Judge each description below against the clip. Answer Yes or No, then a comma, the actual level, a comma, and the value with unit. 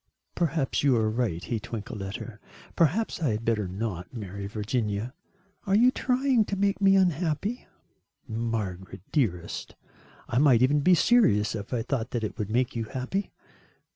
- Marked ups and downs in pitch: Yes, wide, 7.8 semitones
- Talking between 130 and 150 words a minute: No, average, 165 wpm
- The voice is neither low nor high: No, low, 120 Hz